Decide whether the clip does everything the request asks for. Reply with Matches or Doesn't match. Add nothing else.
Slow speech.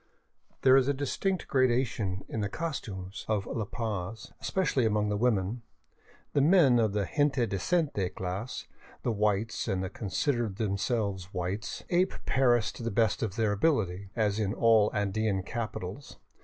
Doesn't match